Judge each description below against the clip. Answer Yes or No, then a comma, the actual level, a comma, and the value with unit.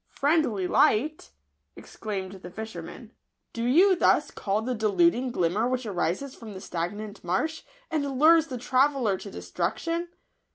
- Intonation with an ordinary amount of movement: No, wide, 6.9 semitones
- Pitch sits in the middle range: No, high, 230 Hz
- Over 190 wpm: No, average, 155 wpm